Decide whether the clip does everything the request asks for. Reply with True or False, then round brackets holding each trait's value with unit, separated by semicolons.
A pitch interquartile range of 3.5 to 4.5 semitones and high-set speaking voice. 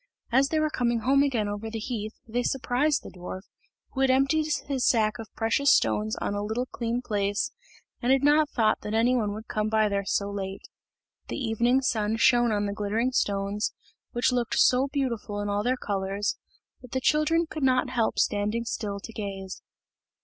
True (4.0 semitones; 225 Hz)